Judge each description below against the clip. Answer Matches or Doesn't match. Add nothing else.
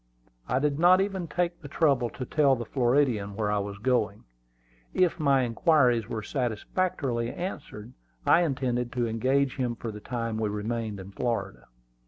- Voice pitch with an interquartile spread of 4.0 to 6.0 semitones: Matches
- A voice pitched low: Matches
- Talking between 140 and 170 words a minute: Matches